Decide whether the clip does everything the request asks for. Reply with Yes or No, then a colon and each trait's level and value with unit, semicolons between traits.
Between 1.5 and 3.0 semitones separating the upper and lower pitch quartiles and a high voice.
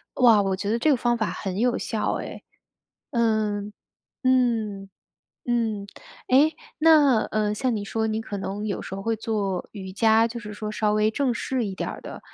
Yes: narrow, 2.6 semitones; high, 220 Hz